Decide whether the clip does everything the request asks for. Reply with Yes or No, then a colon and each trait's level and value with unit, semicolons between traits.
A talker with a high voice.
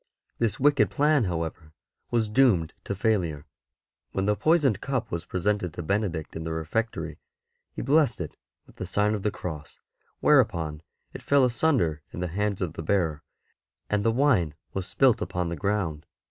No: very low, 95 Hz